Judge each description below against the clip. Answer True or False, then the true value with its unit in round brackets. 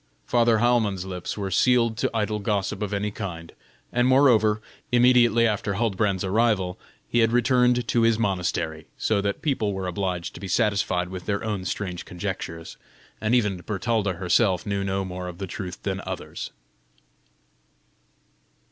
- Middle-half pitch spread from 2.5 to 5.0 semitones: True (3.6 semitones)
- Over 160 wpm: False (155 wpm)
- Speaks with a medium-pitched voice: False (100 Hz)